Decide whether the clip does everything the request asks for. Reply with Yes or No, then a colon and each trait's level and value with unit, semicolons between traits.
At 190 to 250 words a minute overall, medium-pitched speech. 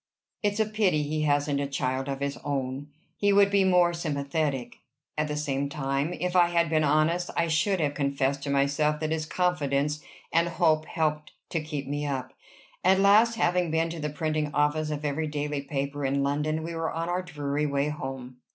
Yes: average, 195 wpm; medium, 150 Hz